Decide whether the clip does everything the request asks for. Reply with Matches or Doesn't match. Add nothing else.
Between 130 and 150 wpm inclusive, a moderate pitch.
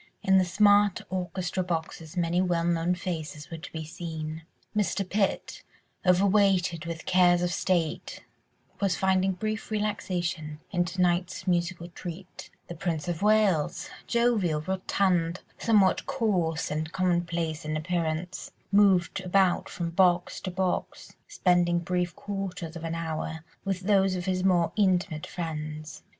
Matches